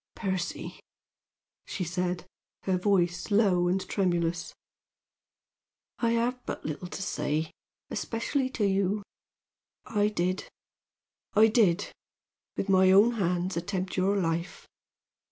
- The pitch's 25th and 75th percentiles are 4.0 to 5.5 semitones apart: No, average, 2.8 semitones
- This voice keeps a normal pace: No, slow, 110 wpm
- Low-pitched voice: No, high, 190 Hz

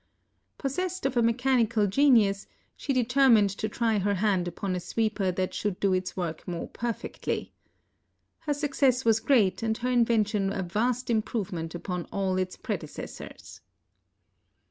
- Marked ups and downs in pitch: No, average, 4.5 semitones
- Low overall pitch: No, high, 215 Hz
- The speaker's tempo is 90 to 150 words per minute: Yes, average, 145 wpm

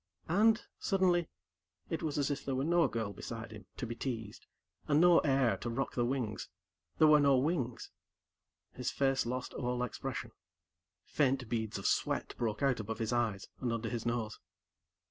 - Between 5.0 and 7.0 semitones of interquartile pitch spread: No, average, 3.9 semitones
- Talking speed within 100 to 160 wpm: No, average, 175 wpm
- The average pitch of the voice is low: Yes, low, 125 Hz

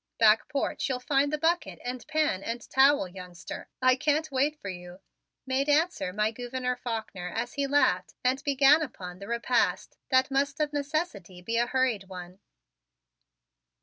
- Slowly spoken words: No, average, 160 wpm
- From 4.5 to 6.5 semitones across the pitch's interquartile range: Yes, average, 5.3 semitones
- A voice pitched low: No, very high, 255 Hz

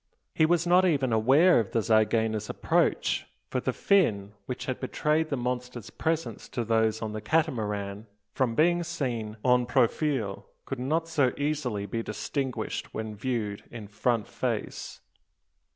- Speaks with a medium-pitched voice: No, low, 125 Hz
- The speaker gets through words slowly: No, average, 150 wpm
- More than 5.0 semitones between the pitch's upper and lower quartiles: Yes, wide, 5.6 semitones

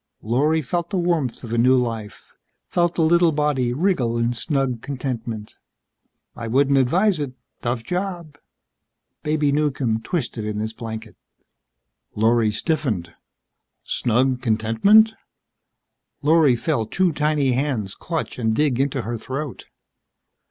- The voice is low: Yes, low, 130 Hz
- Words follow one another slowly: Yes, slow, 125 wpm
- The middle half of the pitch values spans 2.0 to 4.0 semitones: No, average, 5.1 semitones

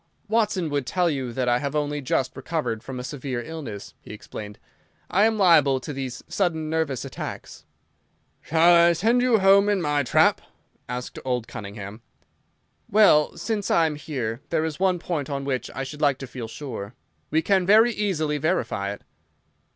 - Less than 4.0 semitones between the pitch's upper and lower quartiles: No, wide, 5.5 semitones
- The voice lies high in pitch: No, medium, 150 Hz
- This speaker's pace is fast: No, average, 175 wpm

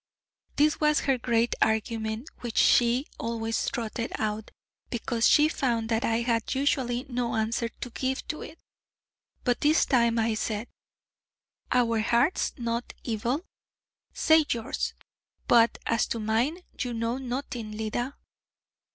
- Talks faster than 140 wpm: No, slow, 135 wpm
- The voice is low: No, high, 235 Hz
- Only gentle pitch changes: Yes, narrow, 2.3 semitones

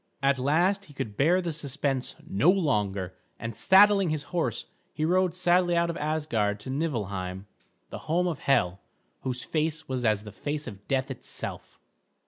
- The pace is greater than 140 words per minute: Yes, average, 165 wpm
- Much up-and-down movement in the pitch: Yes, wide, 6.8 semitones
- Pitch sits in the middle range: Yes, medium, 145 Hz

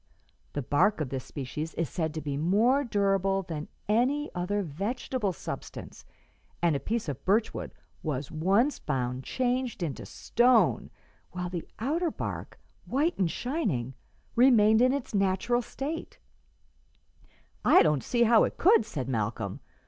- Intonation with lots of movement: Yes, wide, 8.1 semitones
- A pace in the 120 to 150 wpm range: Yes, average, 145 wpm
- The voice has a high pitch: Yes, high, 195 Hz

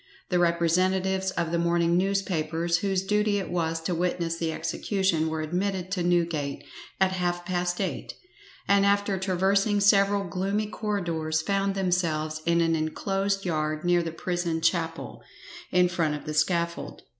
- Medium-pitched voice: Yes, medium, 175 Hz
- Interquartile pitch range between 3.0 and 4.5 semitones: No, narrow, 2.6 semitones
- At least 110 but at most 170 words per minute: Yes, average, 150 wpm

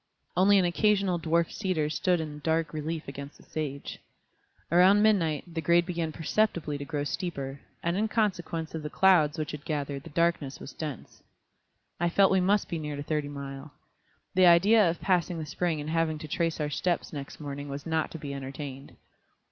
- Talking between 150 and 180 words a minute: No, average, 190 wpm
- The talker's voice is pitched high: No, medium, 160 Hz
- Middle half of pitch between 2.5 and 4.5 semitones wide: Yes, average, 3.1 semitones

